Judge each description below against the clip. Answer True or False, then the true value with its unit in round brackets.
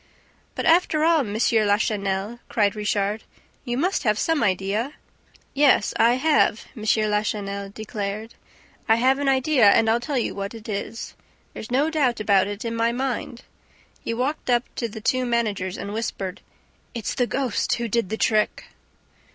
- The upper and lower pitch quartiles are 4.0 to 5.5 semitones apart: False (3.6 semitones)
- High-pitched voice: True (225 Hz)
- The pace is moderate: True (165 wpm)